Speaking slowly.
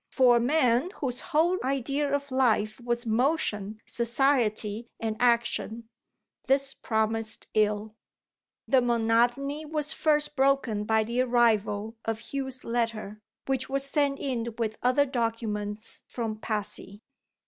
Yes: slow, 125 wpm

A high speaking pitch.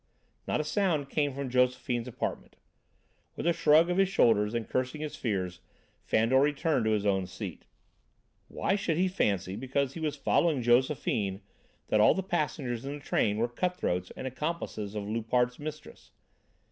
No: low, 130 Hz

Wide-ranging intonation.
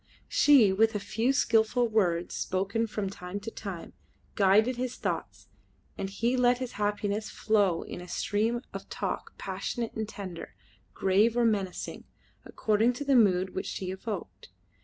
No: average, 3.4 semitones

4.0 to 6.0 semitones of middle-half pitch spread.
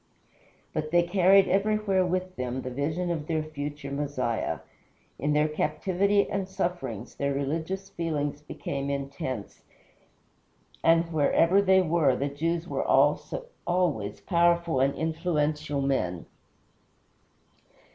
Yes: average, 4.3 semitones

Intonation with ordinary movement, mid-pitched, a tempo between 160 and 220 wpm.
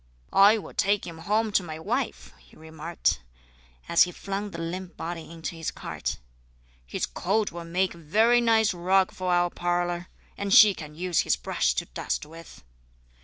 Yes: average, 3.3 semitones; medium, 175 Hz; average, 175 wpm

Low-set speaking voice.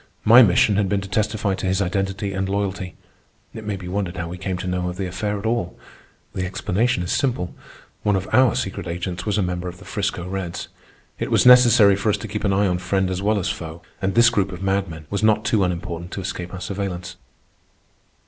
Yes: very low, 95 Hz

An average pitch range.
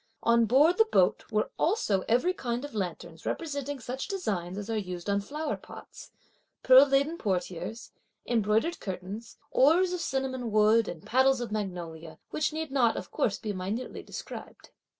No: wide, 5.8 semitones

